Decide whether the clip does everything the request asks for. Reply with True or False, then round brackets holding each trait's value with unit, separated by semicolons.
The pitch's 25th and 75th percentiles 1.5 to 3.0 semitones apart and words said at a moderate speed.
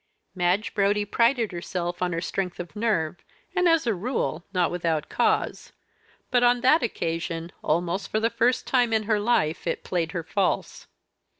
False (5.2 semitones; 170 wpm)